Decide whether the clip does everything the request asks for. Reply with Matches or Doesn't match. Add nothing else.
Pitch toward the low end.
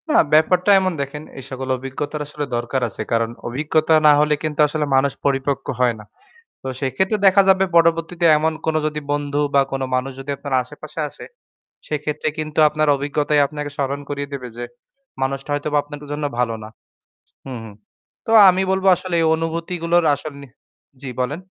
Doesn't match